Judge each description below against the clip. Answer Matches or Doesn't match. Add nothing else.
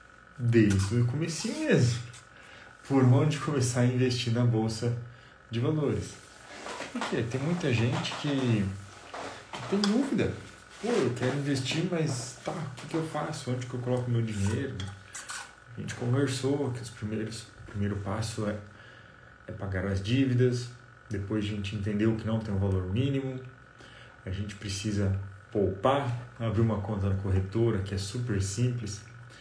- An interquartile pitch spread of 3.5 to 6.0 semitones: Matches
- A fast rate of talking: Doesn't match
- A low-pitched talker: Matches